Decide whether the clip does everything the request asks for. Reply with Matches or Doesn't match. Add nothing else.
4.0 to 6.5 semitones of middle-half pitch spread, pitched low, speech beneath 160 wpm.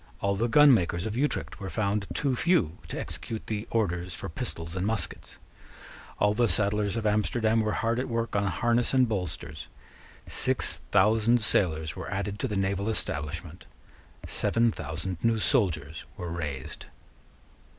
Matches